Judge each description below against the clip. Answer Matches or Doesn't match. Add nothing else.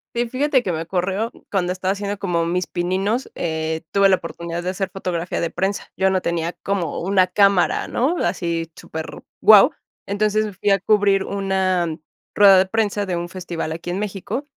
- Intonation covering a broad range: Doesn't match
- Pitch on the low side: Doesn't match